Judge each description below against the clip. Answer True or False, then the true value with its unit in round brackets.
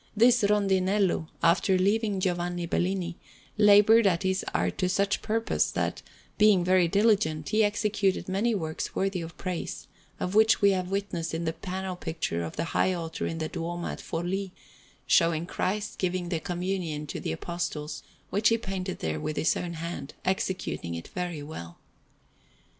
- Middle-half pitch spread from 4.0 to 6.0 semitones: False (3.1 semitones)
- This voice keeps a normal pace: True (165 wpm)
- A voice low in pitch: False (185 Hz)